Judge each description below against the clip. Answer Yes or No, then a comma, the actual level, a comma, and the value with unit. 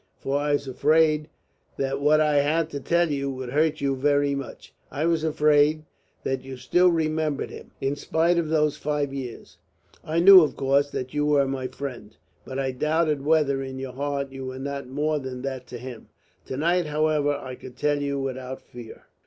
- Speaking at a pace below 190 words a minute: No, average, 195 wpm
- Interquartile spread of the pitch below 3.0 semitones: Yes, narrow, 2.4 semitones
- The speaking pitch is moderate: Yes, medium, 145 Hz